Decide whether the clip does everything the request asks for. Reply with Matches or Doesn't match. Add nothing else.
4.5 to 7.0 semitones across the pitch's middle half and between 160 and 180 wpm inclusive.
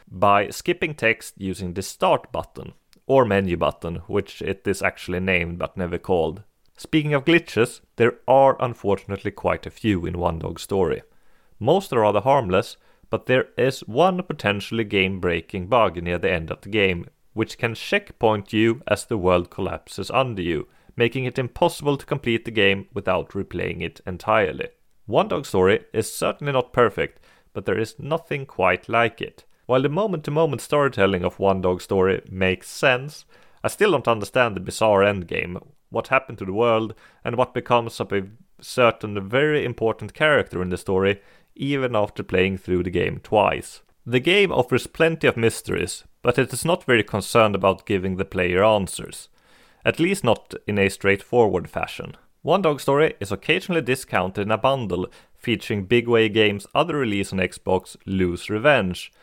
Matches